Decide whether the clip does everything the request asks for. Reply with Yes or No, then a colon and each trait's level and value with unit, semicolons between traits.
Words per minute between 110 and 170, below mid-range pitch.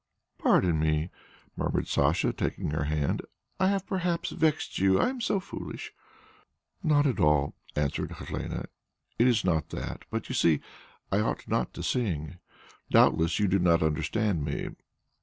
Yes: average, 155 wpm; very low, 90 Hz